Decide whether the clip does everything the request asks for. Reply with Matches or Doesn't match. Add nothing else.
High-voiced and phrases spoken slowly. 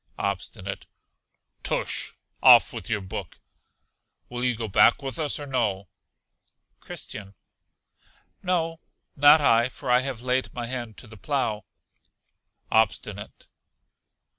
Doesn't match